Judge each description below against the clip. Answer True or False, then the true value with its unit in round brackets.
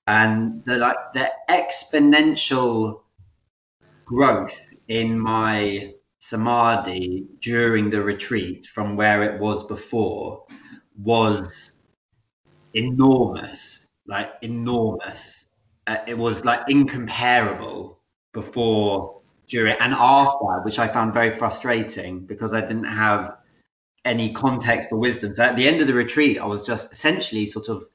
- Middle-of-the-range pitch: False (110 Hz)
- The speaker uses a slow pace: True (120 wpm)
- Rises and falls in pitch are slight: True (2.2 semitones)